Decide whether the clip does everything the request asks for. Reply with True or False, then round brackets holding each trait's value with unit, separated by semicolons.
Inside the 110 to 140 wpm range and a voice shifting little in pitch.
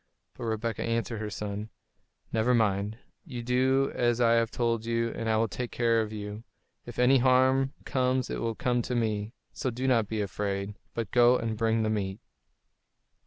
False (185 wpm; 2.2 semitones)